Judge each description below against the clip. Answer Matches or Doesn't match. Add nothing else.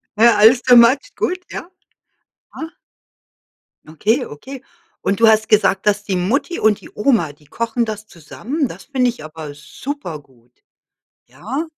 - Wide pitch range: Matches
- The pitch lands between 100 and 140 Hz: Doesn't match